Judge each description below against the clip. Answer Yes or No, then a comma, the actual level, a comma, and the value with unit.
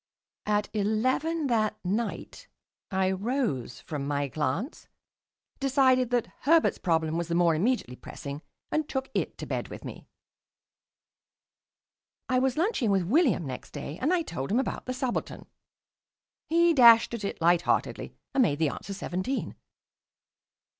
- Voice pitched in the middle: No, high, 220 Hz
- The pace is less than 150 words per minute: Yes, average, 140 wpm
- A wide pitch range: Yes, wide, 7.7 semitones